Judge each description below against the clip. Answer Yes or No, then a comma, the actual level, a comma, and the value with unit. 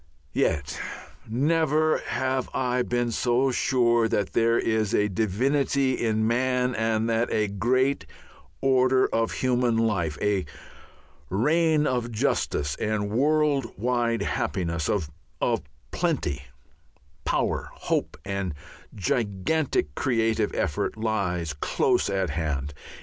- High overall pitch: No, low, 115 Hz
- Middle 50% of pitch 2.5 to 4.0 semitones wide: No, average, 4.6 semitones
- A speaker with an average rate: No, slow, 110 wpm